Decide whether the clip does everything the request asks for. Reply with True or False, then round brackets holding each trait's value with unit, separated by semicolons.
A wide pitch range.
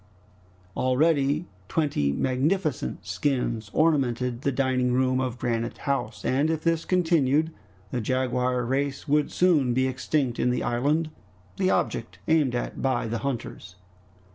False (3.5 semitones)